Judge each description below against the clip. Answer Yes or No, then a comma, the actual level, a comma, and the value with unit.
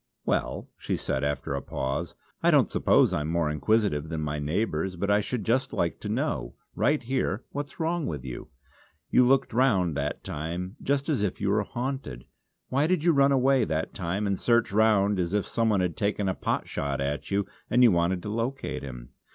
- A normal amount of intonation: No, wide, 8.0 semitones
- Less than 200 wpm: No, fast, 205 wpm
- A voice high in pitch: No, low, 100 Hz